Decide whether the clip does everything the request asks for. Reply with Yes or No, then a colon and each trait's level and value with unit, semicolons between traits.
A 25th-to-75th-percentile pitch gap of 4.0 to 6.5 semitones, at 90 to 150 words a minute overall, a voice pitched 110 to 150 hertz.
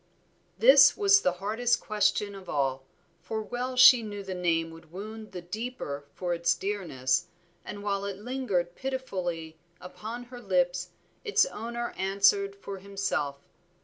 No: average, 4.6 semitones; average, 145 wpm; high, 200 Hz